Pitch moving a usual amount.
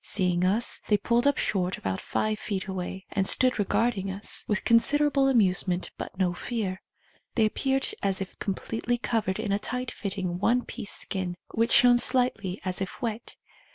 Yes: average, 4.2 semitones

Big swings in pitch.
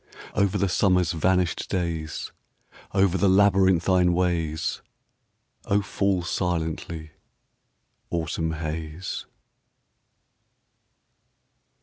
No: narrow, 2.6 semitones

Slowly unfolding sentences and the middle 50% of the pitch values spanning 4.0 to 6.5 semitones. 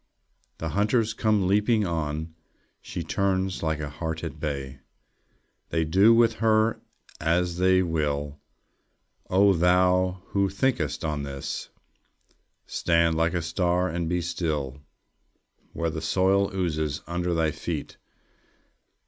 No: slow, 125 wpm; average, 3.3 semitones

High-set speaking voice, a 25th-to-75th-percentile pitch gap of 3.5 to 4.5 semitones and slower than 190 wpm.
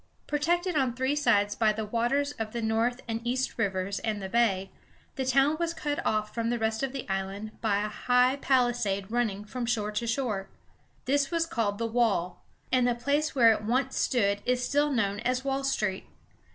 No: high, 235 Hz; average, 4.0 semitones; average, 195 wpm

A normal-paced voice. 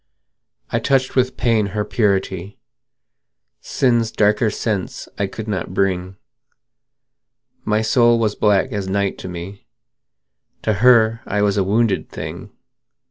No: slow, 130 wpm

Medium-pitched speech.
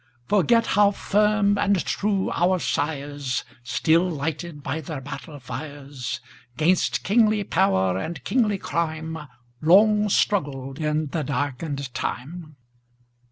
Yes: medium, 160 Hz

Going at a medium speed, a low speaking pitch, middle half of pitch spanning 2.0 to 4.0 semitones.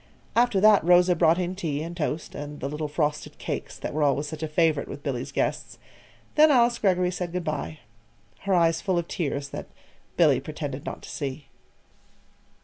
No: average, 185 wpm; medium, 165 Hz; average, 3.6 semitones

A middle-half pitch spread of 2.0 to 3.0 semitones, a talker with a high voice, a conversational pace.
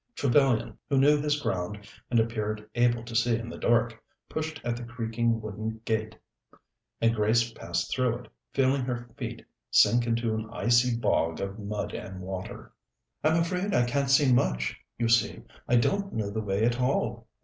No: narrow, 2.5 semitones; low, 115 Hz; average, 175 wpm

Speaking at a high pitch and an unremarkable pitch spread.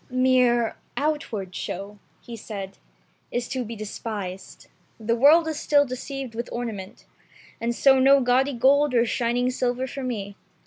Yes: high, 245 Hz; average, 3.1 semitones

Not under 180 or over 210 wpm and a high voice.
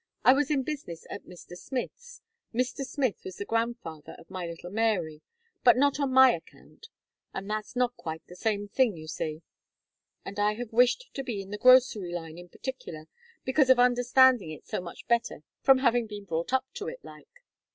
Yes: average, 195 wpm; high, 230 Hz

